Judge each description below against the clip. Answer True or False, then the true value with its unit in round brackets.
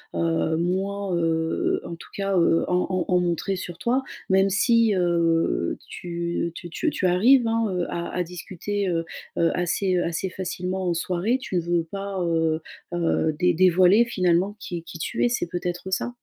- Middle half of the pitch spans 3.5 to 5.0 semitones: False (2.5 semitones)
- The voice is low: False (180 Hz)